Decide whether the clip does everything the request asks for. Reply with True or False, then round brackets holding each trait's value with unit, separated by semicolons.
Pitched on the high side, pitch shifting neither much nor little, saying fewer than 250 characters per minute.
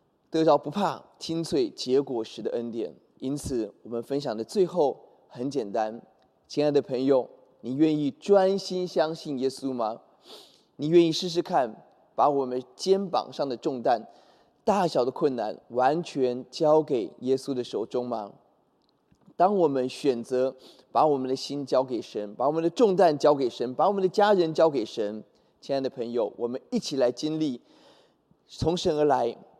False (140 Hz; 4.6 semitones; 235 characters per minute)